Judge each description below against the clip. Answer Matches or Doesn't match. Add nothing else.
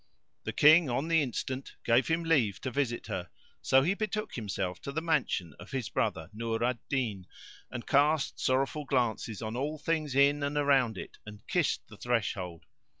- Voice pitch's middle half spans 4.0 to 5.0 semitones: Matches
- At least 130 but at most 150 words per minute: Doesn't match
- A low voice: Matches